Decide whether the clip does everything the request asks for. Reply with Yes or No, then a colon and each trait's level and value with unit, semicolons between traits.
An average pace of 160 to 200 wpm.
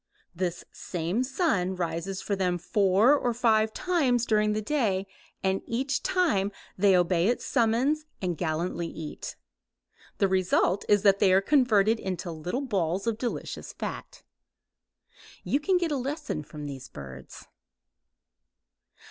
No: average, 140 wpm